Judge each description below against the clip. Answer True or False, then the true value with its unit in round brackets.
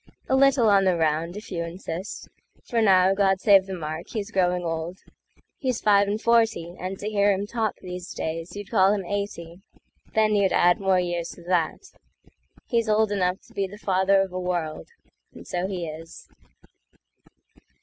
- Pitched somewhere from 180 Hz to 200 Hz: True (190 Hz)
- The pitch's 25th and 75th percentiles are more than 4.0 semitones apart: False (2.8 semitones)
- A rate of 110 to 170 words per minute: True (160 wpm)